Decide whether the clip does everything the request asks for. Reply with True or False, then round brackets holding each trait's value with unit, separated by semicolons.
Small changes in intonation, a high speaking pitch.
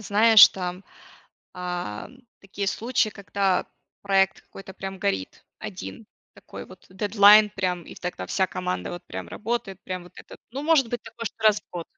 False (3.0 semitones; 195 Hz)